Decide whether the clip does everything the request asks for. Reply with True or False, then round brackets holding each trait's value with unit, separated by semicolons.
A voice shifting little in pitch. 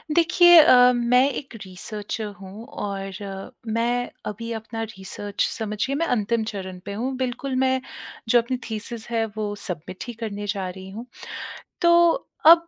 False (4.1 semitones)